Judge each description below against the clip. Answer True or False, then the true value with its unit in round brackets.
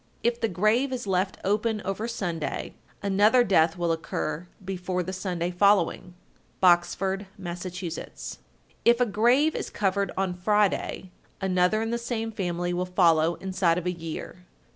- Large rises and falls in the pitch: False (3.1 semitones)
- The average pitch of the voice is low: False (190 Hz)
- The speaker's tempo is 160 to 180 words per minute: False (150 wpm)